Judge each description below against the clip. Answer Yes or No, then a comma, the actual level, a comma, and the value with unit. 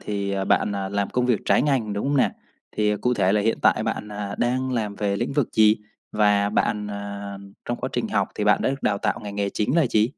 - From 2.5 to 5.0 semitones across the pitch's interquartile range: Yes, average, 2.9 semitones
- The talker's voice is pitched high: No, low, 105 Hz